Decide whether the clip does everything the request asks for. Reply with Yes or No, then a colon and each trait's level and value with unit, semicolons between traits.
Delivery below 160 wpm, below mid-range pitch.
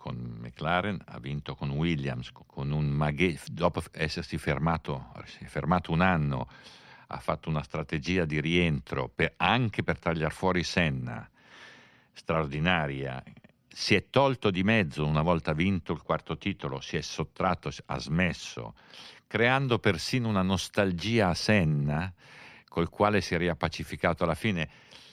Yes: average, 135 wpm; very low, 85 Hz